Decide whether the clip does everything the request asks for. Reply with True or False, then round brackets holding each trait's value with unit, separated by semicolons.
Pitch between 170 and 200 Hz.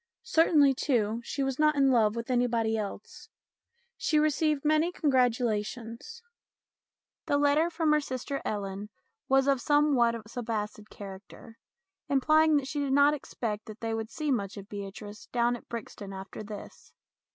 False (245 Hz)